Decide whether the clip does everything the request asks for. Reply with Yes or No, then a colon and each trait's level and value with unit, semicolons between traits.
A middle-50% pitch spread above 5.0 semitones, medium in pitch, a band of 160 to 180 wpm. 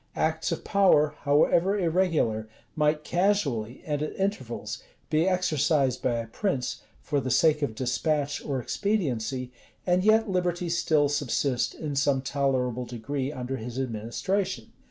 No: wide, 5.4 semitones; medium, 145 Hz; slow, 135 wpm